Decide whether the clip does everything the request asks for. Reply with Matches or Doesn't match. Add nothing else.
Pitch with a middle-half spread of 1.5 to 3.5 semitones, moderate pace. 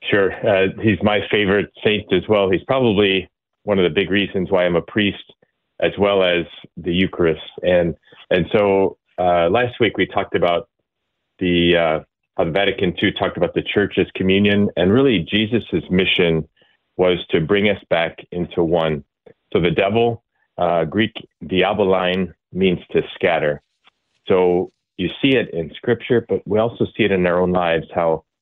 Matches